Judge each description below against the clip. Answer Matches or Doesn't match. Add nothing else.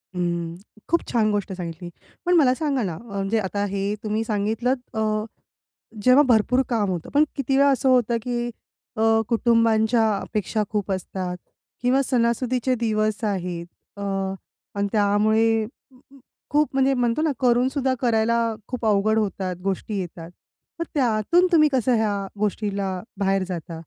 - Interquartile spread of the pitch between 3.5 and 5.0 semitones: Matches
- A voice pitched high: Matches